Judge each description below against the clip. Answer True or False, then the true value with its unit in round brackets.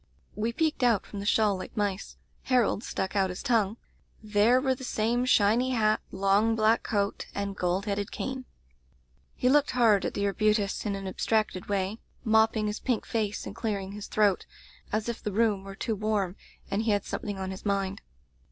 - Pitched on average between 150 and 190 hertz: False (210 Hz)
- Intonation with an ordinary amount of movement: False (2.3 semitones)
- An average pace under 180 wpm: False (190 wpm)